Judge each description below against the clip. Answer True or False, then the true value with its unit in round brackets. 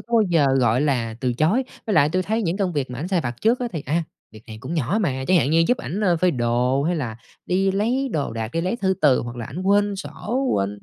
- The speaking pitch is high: False (165 Hz)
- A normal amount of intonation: False (7.2 semitones)